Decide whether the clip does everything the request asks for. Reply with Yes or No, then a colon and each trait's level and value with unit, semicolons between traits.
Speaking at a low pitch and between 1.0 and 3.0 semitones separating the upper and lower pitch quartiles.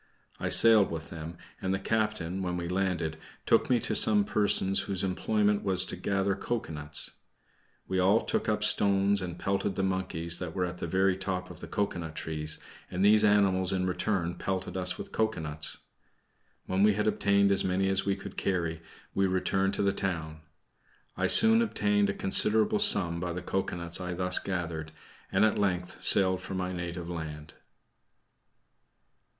Yes: very low, 95 Hz; narrow, 2.4 semitones